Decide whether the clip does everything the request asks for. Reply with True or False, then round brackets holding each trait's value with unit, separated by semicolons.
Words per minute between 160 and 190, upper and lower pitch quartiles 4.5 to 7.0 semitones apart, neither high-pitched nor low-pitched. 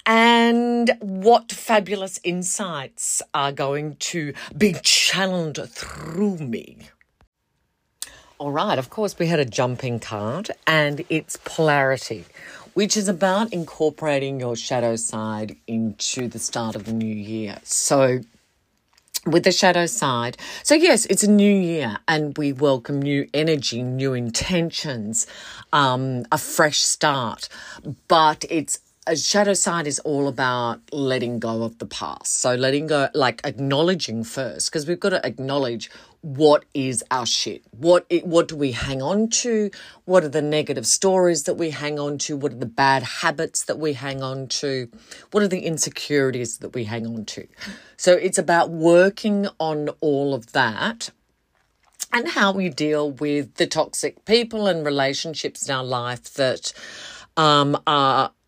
False (150 wpm; 5.1 semitones; 150 Hz)